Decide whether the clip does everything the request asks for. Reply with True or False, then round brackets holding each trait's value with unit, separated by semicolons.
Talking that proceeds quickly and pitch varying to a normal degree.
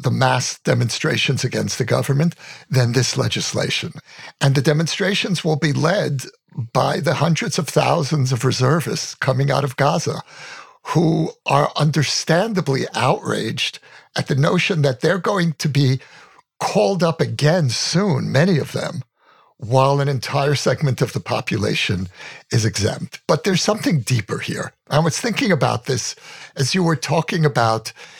False (145 wpm; 4.1 semitones)